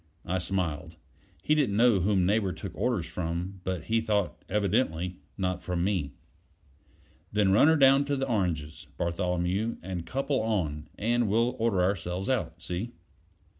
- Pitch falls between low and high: No, very low, 95 Hz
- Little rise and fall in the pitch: No, average, 4.4 semitones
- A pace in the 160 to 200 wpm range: No, average, 150 wpm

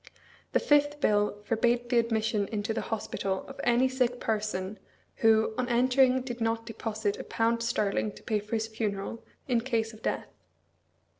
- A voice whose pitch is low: No, high, 225 Hz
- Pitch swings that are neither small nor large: No, narrow, 2.1 semitones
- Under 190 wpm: Yes, average, 165 wpm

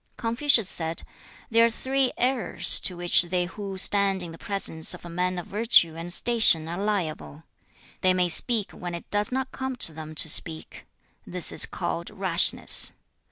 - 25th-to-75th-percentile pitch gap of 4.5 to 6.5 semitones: Yes, average, 4.9 semitones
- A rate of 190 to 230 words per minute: No, average, 175 wpm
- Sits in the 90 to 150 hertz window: No, medium, 185 Hz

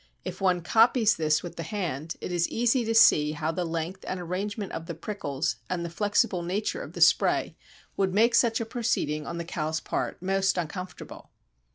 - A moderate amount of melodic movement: Yes, average, 4.1 semitones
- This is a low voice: No, medium, 180 Hz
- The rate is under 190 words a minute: No, average, 195 wpm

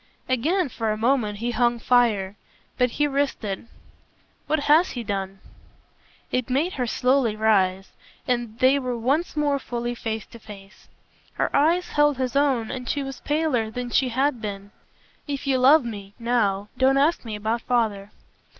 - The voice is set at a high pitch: Yes, high, 245 Hz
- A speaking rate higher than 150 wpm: Yes, average, 170 wpm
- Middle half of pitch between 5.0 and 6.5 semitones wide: No, average, 4.1 semitones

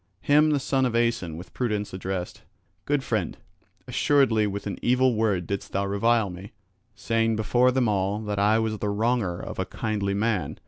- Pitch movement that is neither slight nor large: Yes, average, 3.3 semitones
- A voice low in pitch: Yes, low, 110 Hz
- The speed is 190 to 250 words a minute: No, average, 180 wpm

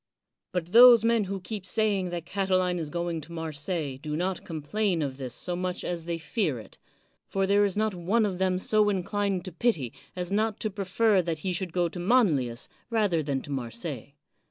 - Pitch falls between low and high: Yes, medium, 180 Hz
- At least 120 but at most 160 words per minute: No, fast, 205 wpm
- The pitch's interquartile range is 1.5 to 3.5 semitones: No, average, 4.0 semitones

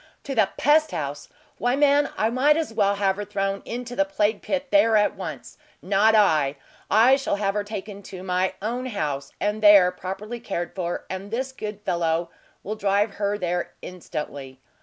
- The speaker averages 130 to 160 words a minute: No, average, 180 wpm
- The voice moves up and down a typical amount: Yes, average, 4.1 semitones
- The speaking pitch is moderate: No, high, 205 Hz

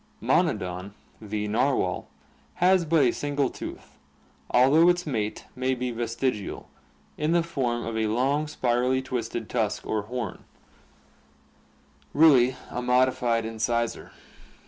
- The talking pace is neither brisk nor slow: No, slow, 120 wpm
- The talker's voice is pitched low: Yes, low, 125 Hz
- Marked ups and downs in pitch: No, average, 3.7 semitones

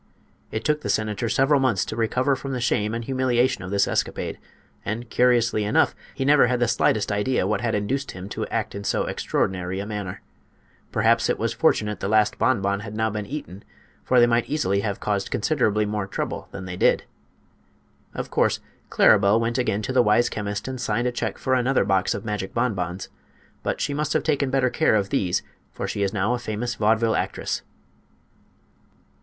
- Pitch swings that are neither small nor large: Yes, average, 3.7 semitones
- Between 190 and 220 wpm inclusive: Yes, average, 195 wpm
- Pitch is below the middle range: Yes, low, 110 Hz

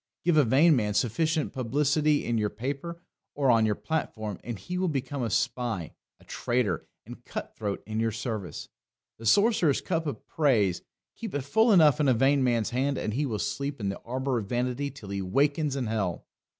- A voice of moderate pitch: No, low, 130 Hz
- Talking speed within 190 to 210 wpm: Yes, average, 200 wpm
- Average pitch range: Yes, average, 5.0 semitones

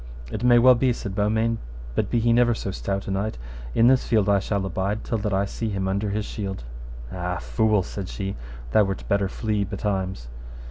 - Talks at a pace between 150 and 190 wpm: No, fast, 205 wpm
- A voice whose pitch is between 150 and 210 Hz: No, low, 100 Hz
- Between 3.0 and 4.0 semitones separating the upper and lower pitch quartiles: No, narrow, 2.5 semitones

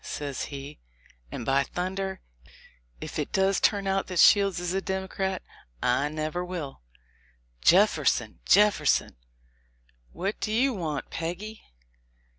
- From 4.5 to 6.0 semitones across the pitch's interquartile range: Yes, average, 5.1 semitones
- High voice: No, medium, 180 Hz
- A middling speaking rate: No, slow, 125 wpm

